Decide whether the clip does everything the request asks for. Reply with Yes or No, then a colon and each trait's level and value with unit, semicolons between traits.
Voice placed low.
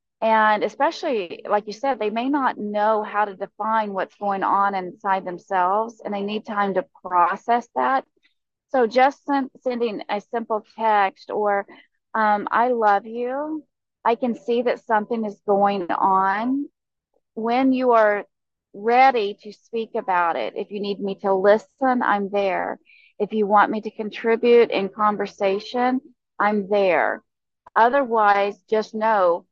No: high, 215 Hz